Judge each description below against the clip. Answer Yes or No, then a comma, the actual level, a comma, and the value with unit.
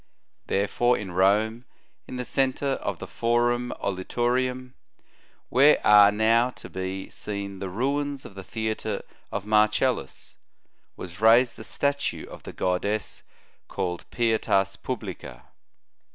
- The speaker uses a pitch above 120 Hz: No, low, 110 Hz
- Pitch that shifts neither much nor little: Yes, average, 4.1 semitones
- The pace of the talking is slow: Yes, slow, 125 wpm